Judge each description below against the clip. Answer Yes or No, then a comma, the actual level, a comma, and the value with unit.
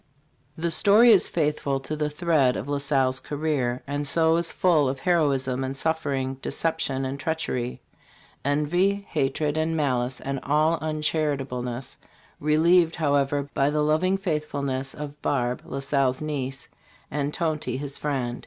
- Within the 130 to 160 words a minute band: Yes, average, 145 wpm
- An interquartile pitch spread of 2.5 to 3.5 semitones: Yes, average, 2.8 semitones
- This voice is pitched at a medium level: Yes, medium, 145 Hz